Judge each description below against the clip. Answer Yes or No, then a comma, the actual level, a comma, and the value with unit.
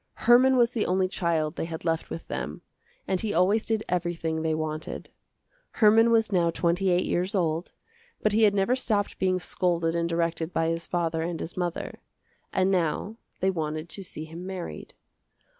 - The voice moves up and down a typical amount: Yes, average, 3.3 semitones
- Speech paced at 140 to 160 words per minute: No, average, 180 wpm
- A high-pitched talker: No, medium, 175 Hz